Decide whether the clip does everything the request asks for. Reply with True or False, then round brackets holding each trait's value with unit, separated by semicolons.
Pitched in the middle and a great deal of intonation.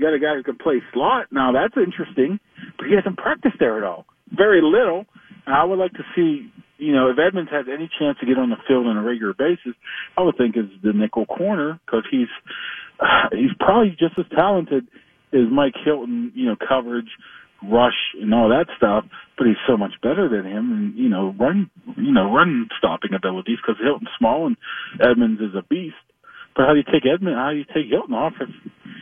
True (160 Hz; 8.4 semitones)